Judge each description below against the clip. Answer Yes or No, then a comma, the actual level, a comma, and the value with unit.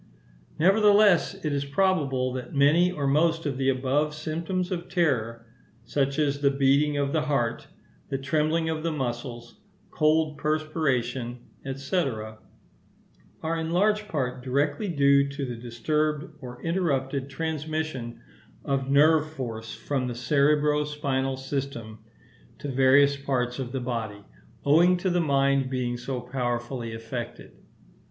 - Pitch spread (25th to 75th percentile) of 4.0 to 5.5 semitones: No, average, 3.4 semitones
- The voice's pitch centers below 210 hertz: Yes, medium, 140 Hz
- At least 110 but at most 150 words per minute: Yes, slow, 135 wpm